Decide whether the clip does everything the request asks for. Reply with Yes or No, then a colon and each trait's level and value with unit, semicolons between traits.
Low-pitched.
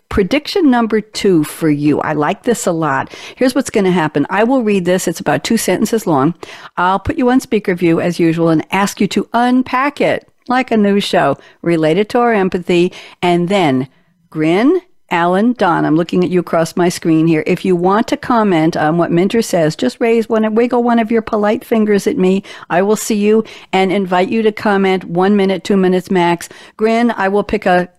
No: high, 195 Hz